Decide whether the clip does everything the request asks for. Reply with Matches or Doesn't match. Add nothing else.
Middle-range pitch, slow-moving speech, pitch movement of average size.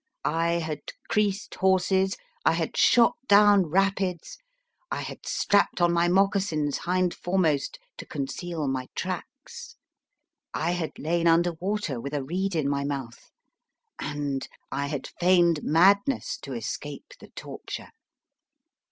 Matches